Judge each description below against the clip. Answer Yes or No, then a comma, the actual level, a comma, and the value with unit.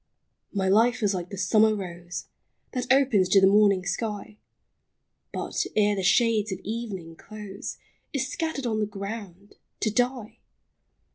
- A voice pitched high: Yes, high, 210 Hz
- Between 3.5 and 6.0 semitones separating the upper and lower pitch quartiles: No, average, 3.1 semitones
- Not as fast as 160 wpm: Yes, average, 150 wpm